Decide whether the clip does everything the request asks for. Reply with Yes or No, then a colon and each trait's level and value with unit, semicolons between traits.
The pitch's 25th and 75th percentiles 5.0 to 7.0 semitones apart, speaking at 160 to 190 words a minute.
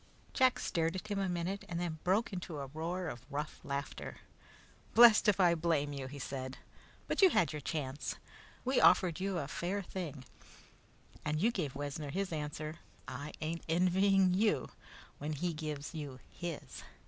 No: average, 4.3 semitones; average, 170 wpm